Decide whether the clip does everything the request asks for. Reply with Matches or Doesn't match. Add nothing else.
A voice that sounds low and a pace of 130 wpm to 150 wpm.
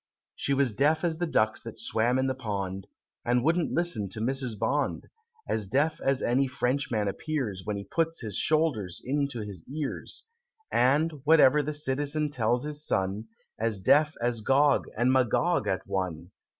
Doesn't match